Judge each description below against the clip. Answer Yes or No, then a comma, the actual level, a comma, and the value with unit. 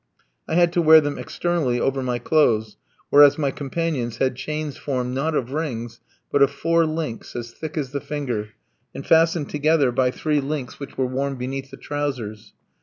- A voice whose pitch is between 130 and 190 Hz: Yes, medium, 140 Hz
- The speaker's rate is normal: Yes, average, 180 wpm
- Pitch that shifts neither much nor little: Yes, average, 3.5 semitones